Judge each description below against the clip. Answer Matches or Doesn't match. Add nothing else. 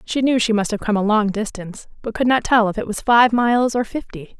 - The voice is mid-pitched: Doesn't match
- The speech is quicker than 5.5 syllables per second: Matches